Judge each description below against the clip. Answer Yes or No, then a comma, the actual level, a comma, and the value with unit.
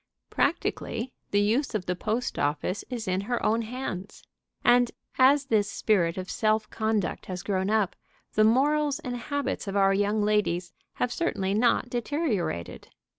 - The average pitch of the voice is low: No, high, 215 Hz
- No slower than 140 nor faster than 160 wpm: Yes, average, 155 wpm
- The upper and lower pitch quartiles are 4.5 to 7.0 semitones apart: No, average, 4.1 semitones